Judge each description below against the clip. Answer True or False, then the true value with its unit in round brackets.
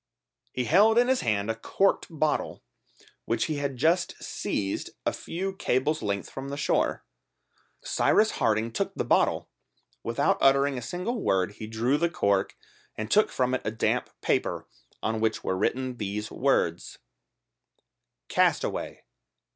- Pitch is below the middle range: True (130 Hz)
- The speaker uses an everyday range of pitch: False (6.6 semitones)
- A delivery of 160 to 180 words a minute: False (145 wpm)